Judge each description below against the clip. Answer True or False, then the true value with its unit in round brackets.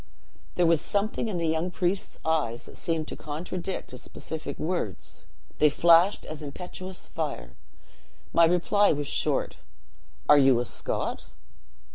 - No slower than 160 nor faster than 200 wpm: False (140 wpm)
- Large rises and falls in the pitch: False (3.5 semitones)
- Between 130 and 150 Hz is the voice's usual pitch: False (165 Hz)